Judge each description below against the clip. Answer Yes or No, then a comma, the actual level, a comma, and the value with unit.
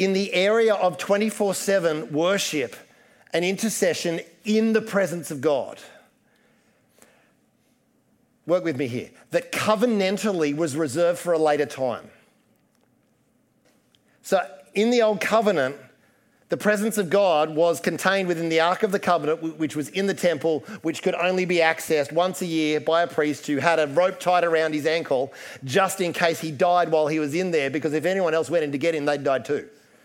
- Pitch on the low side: No, medium, 170 Hz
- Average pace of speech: Yes, average, 175 wpm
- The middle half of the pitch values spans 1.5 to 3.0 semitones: No, average, 3.5 semitones